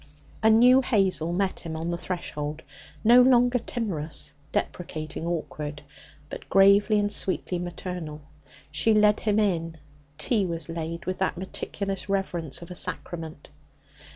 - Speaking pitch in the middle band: Yes, medium, 180 Hz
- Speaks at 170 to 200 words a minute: No, slow, 135 wpm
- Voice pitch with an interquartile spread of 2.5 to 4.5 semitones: Yes, average, 4.1 semitones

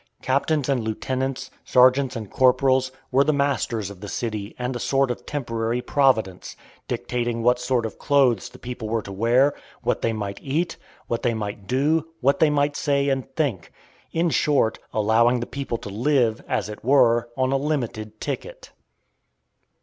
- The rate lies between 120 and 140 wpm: No, average, 170 wpm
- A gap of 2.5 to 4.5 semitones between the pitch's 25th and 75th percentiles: Yes, average, 3.6 semitones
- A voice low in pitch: Yes, low, 125 Hz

